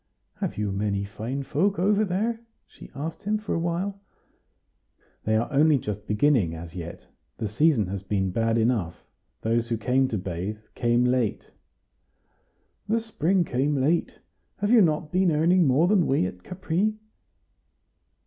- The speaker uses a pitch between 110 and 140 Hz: Yes, low, 135 Hz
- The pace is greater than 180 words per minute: No, average, 155 wpm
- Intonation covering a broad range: Yes, wide, 8.9 semitones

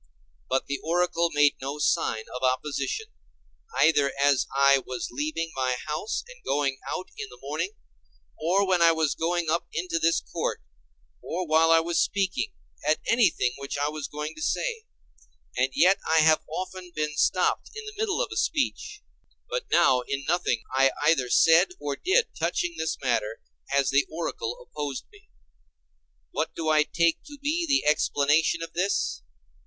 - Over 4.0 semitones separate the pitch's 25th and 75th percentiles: Yes, average, 4.6 semitones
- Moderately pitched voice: Yes, medium, 160 Hz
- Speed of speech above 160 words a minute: Yes, average, 170 wpm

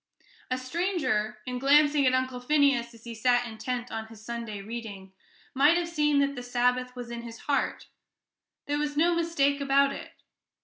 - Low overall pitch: No, very high, 255 Hz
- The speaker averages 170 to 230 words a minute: Yes, average, 175 wpm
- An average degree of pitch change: Yes, average, 3.5 semitones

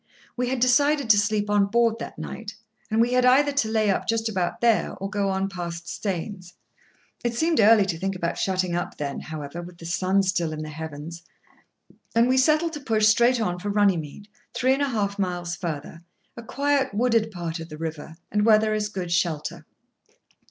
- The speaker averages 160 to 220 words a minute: Yes, average, 200 wpm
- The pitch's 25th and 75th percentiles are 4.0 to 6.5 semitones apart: Yes, average, 5.0 semitones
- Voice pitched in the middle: No, high, 205 Hz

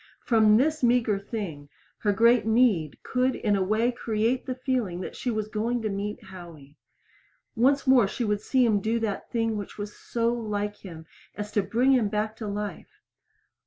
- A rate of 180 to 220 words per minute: Yes, average, 185 wpm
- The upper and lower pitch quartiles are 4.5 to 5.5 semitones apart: No, average, 2.9 semitones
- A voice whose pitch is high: Yes, high, 215 Hz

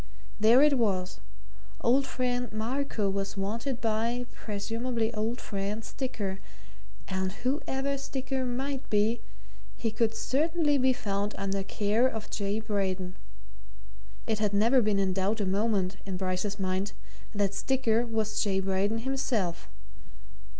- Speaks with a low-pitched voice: No, high, 220 Hz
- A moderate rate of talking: No, slow, 130 wpm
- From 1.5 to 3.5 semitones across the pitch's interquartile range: No, average, 3.9 semitones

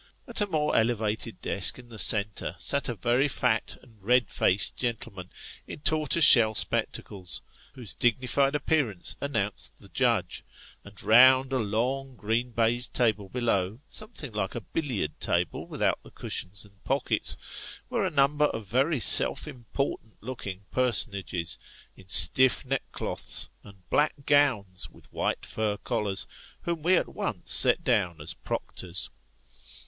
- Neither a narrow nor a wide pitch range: Yes, average, 4.9 semitones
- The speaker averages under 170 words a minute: Yes, average, 145 wpm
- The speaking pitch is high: No, low, 115 Hz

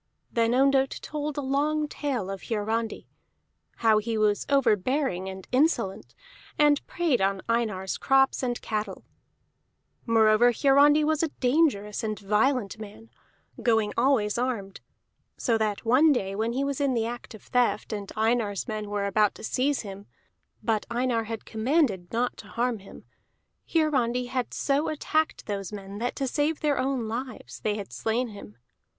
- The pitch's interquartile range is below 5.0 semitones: Yes, average, 4.4 semitones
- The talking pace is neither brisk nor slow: Yes, average, 155 wpm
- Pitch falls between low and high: No, high, 235 Hz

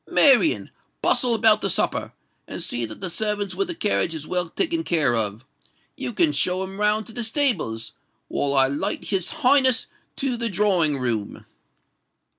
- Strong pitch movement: Yes, wide, 8.8 semitones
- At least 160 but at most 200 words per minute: Yes, average, 165 wpm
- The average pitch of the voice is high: Yes, high, 200 Hz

